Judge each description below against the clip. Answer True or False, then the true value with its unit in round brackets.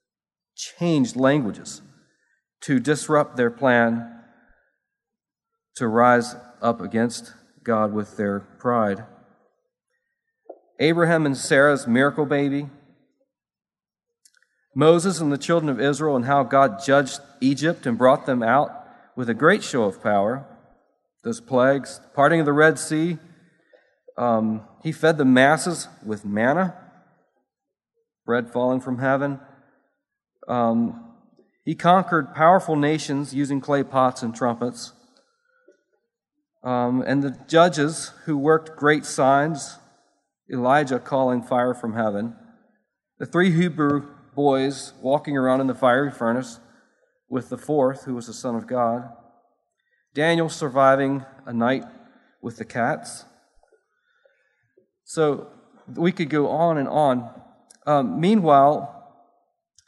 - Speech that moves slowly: True (115 wpm)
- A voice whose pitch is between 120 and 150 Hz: True (140 Hz)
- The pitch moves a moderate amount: True (4.6 semitones)